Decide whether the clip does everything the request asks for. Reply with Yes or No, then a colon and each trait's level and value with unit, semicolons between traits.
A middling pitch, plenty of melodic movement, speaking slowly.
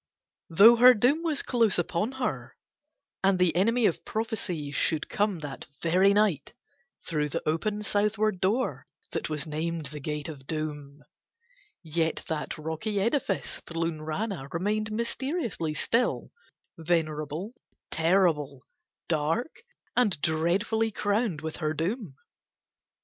Yes: medium, 175 Hz; wide, 5.7 semitones; slow, 120 wpm